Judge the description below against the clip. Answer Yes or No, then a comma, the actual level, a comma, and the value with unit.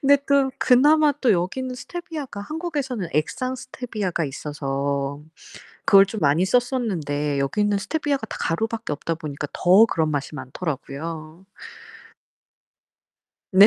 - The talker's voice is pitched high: Yes, high, 195 Hz